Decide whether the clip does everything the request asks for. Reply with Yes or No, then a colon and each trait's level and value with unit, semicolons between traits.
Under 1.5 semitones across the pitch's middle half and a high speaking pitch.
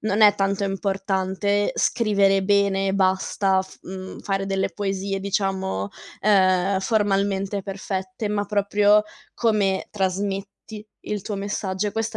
Yes: narrow, 1.1 semitones; high, 195 Hz